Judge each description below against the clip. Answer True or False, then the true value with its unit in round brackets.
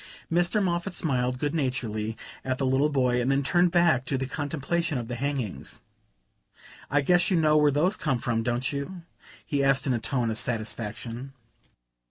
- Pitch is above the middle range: False (135 Hz)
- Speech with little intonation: False (4.3 semitones)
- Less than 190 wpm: True (180 wpm)